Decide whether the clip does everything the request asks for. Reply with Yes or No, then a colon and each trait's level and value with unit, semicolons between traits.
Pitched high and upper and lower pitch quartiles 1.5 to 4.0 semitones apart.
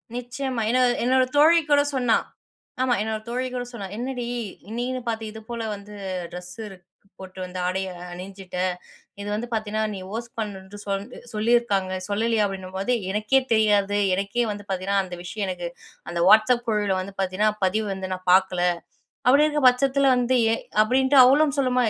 No: high, 215 Hz; average, 4.4 semitones